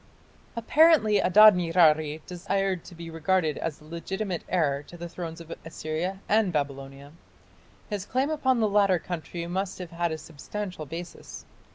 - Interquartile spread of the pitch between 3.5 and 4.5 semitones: Yes, average, 3.8 semitones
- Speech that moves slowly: No, average, 155 wpm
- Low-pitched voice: No, medium, 175 Hz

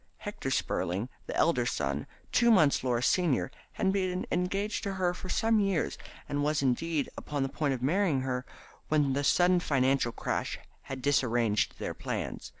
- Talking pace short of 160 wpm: No, average, 165 wpm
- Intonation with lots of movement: Yes, wide, 6.0 semitones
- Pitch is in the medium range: Yes, medium, 145 Hz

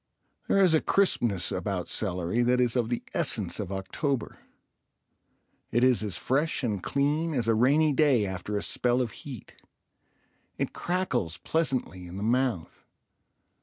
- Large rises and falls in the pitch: Yes, wide, 5.7 semitones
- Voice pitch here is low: Yes, low, 120 Hz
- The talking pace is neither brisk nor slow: Yes, average, 150 wpm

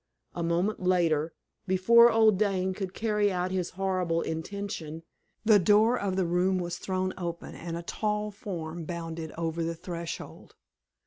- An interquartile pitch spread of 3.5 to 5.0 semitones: No, average, 3.1 semitones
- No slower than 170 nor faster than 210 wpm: No, average, 150 wpm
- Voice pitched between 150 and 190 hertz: Yes, medium, 185 Hz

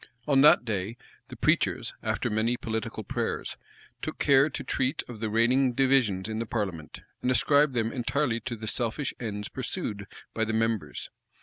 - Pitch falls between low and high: No, low, 115 Hz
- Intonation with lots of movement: No, average, 3.3 semitones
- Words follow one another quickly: No, average, 170 wpm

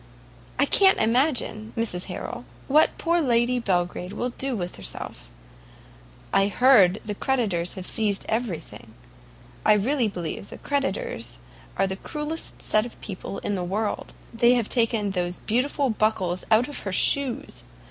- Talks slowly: No, average, 145 wpm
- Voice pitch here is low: No, high, 220 Hz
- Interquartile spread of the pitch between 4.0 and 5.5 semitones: Yes, average, 5.1 semitones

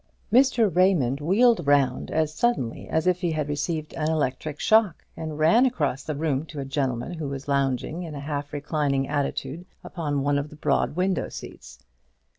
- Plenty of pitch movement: No, average, 3.4 semitones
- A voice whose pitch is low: No, medium, 150 Hz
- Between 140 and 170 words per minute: No, average, 180 wpm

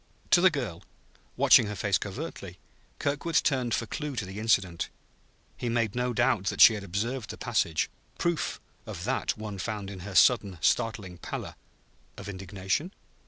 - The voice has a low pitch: Yes, low, 110 Hz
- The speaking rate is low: No, average, 165 wpm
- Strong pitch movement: No, average, 4.5 semitones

